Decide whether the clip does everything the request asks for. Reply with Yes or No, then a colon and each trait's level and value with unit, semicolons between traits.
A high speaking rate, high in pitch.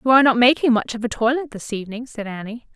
Yes: fast, 260 wpm; high, 235 Hz